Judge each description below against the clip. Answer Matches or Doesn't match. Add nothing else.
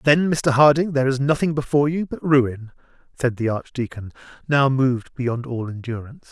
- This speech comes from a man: Matches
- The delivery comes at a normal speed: Matches